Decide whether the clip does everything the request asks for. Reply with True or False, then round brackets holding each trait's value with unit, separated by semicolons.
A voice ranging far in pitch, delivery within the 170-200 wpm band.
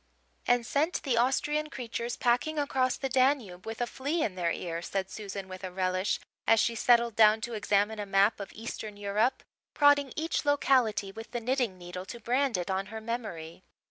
False (4.7 semitones; 190 wpm)